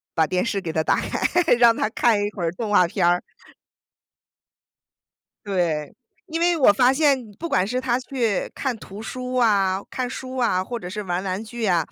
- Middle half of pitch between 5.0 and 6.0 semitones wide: Yes, wide, 5.5 semitones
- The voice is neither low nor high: No, high, 215 Hz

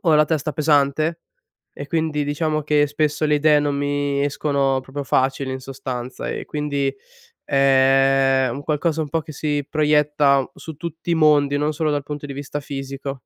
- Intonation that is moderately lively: No, narrow, 1.8 semitones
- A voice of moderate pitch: Yes, medium, 145 Hz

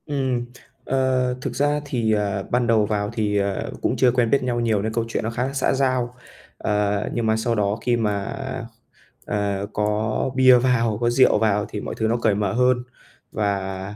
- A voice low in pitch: Yes, low, 115 Hz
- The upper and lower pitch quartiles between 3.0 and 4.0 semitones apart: Yes, average, 3.3 semitones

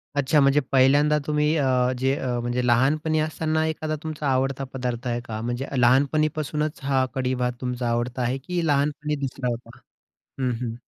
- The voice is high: No, low, 135 Hz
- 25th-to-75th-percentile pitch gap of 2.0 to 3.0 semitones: No, average, 3.4 semitones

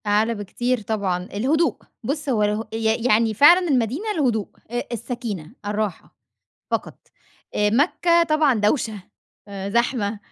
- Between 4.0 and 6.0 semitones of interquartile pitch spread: Yes, average, 4.3 semitones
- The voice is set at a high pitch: Yes, high, 225 Hz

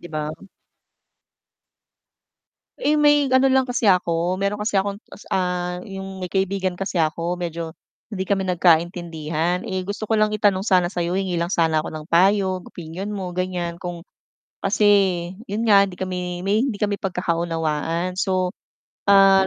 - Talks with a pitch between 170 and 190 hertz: Yes, medium, 185 Hz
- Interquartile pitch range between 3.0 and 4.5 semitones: No, narrow, 2.5 semitones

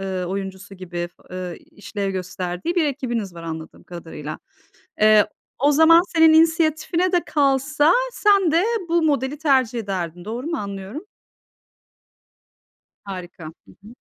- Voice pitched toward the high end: Yes, high, 220 Hz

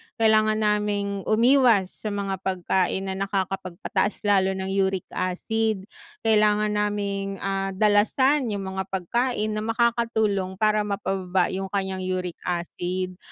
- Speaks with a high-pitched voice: Yes, high, 200 Hz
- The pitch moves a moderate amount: No, narrow, 2.0 semitones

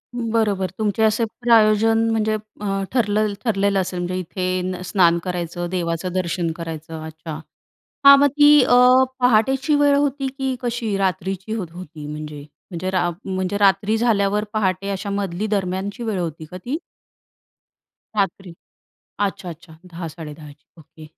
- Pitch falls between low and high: No, high, 195 Hz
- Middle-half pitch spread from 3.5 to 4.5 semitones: Yes, average, 4.1 semitones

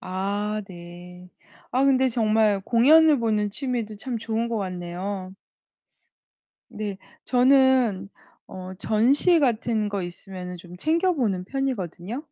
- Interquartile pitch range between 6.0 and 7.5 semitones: No, average, 5.2 semitones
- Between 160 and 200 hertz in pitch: No, high, 215 Hz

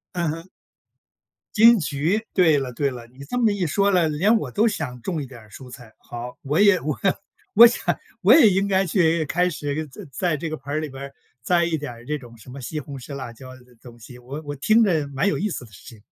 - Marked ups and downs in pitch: Yes, wide, 5.9 semitones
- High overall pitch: No, medium, 150 Hz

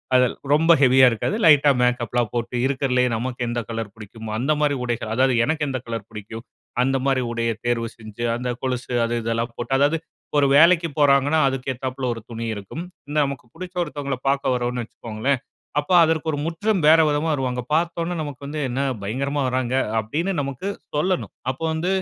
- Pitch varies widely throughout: No, average, 3.8 semitones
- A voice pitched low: Yes, low, 130 Hz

